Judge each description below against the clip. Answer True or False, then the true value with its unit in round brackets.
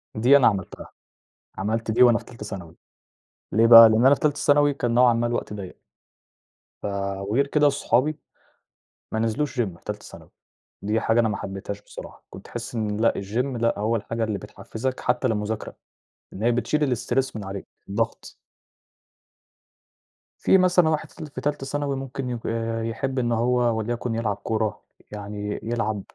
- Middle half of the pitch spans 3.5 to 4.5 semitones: True (3.8 semitones)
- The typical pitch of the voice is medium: False (115 Hz)